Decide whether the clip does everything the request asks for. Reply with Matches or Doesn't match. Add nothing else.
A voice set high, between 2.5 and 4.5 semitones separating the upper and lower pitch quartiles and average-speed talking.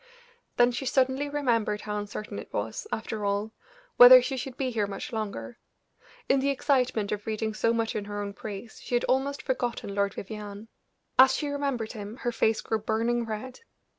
Matches